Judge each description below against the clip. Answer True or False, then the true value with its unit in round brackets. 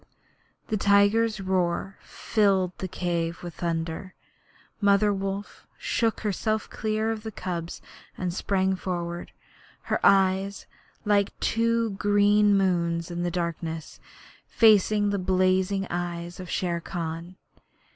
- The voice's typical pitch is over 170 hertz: True (190 Hz)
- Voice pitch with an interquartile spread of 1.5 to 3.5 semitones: True (2.9 semitones)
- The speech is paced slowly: True (115 wpm)